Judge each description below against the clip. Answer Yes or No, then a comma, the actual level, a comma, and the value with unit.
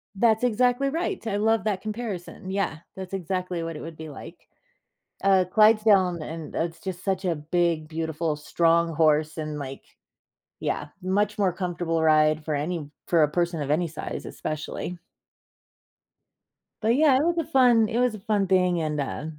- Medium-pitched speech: Yes, medium, 180 Hz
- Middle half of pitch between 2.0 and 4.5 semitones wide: No, average, 4.9 semitones